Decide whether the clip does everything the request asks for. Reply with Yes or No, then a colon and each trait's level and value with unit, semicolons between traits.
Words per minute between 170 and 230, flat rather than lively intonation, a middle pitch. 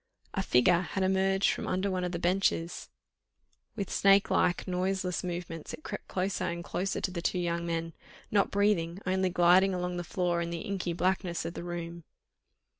Yes: average, 185 wpm; narrow, 1.8 semitones; medium, 180 Hz